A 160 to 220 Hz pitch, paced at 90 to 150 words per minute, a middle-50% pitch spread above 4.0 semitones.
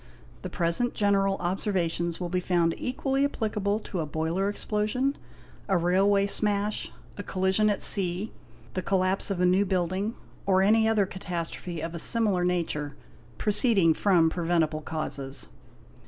No: high, 190 Hz; average, 140 wpm; average, 3.1 semitones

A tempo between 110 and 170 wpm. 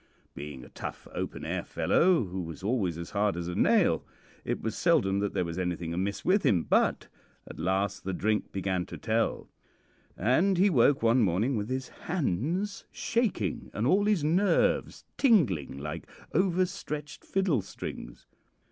Yes: average, 165 wpm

